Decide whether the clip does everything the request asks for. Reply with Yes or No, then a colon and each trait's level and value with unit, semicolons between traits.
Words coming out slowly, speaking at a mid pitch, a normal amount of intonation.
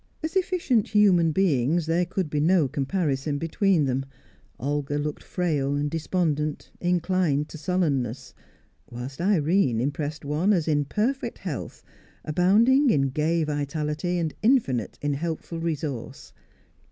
Yes: slow, 120 wpm; medium, 155 Hz; average, 4.1 semitones